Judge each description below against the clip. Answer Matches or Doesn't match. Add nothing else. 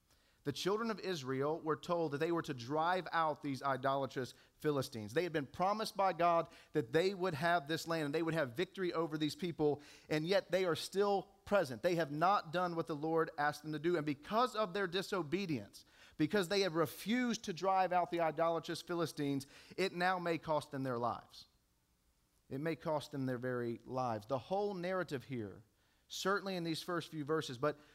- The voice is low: Doesn't match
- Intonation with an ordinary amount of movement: Matches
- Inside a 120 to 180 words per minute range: Doesn't match